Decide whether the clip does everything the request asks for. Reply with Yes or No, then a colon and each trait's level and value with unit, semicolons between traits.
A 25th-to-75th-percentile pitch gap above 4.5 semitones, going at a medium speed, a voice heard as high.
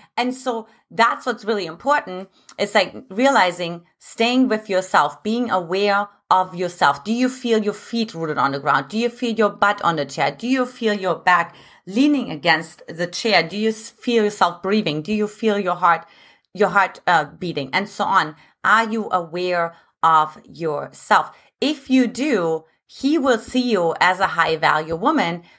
Yes: average, 5.2 semitones; average, 180 wpm; high, 205 Hz